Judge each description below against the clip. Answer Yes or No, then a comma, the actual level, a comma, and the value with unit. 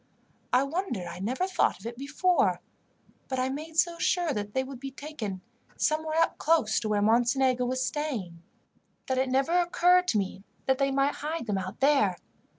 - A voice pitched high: Yes, very high, 265 Hz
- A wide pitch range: Yes, wide, 5.8 semitones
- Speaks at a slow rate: No, average, 180 wpm